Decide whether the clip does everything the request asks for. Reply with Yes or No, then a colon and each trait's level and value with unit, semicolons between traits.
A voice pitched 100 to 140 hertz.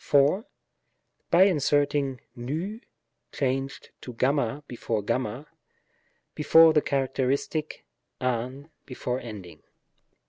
Yes: low, 135 Hz